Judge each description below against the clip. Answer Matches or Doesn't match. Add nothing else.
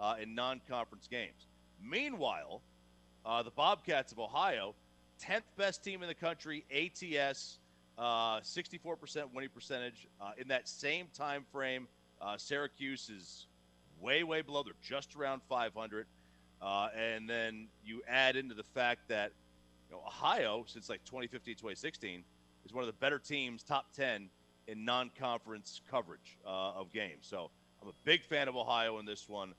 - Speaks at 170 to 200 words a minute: Doesn't match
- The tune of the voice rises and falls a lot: Matches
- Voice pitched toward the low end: Matches